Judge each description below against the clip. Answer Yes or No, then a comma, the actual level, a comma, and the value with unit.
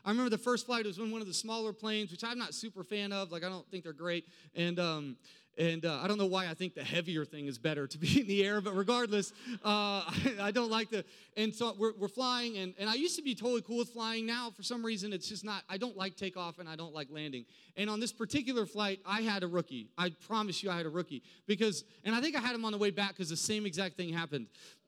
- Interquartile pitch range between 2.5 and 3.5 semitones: No, average, 4.2 semitones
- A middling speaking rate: No, fast, 280 wpm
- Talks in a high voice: Yes, high, 205 Hz